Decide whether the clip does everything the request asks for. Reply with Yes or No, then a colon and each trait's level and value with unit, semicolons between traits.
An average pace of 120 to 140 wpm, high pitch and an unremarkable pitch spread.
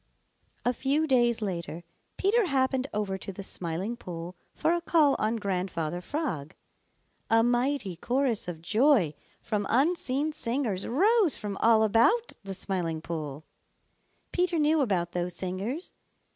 No: slow, 135 wpm; high, 225 Hz; wide, 7.5 semitones